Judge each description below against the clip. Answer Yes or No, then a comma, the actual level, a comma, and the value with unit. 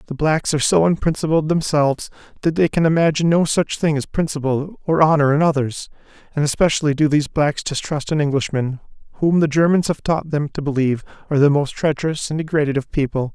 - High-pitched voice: No, medium, 150 Hz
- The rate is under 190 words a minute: No, average, 195 wpm